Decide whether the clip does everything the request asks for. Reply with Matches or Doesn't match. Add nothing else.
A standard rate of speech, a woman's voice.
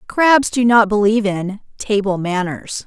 Matches